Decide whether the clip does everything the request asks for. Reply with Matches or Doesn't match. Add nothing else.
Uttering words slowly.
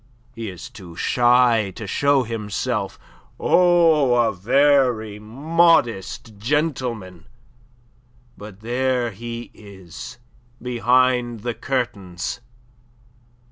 Matches